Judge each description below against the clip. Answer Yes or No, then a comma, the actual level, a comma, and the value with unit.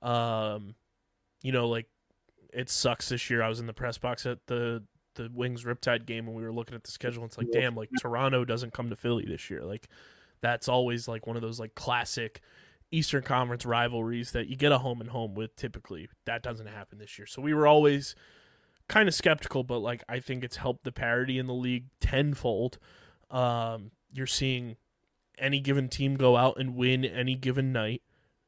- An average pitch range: No, narrow, 2.0 semitones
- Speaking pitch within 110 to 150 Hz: Yes, low, 120 Hz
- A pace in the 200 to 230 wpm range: Yes, fast, 205 wpm